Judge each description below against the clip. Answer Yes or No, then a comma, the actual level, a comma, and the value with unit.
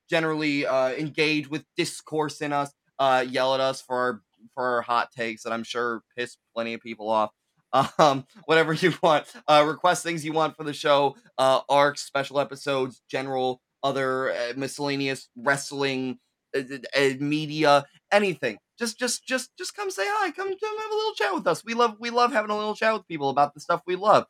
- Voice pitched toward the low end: No, medium, 145 Hz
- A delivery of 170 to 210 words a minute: Yes, average, 200 wpm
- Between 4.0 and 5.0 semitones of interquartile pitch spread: Yes, average, 4.6 semitones